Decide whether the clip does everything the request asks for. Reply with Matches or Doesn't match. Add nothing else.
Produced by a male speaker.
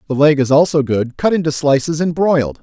Matches